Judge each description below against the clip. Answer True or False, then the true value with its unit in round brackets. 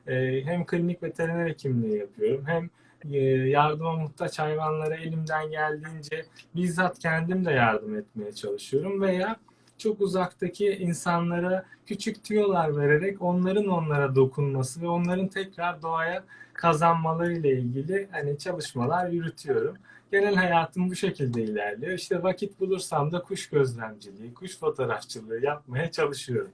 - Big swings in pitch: False (4.2 semitones)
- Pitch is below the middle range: False (170 Hz)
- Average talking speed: True (120 wpm)